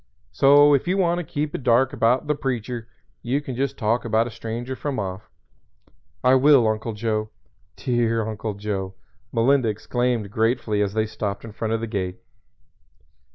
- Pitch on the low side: Yes, low, 115 Hz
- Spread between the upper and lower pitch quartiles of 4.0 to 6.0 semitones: No, average, 3.4 semitones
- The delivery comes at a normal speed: Yes, average, 170 wpm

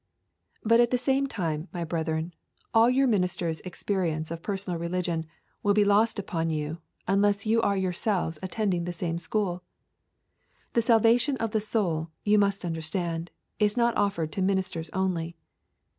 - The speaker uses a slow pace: No, average, 160 wpm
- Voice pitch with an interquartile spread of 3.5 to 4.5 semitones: Yes, average, 4.2 semitones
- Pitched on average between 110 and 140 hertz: No, high, 190 Hz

